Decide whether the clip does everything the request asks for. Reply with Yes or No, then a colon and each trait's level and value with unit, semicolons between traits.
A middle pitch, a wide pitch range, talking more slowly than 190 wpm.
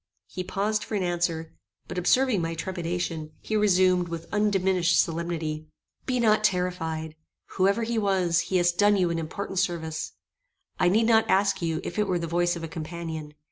No: medium, 180 Hz; average, 3.1 semitones; average, 180 wpm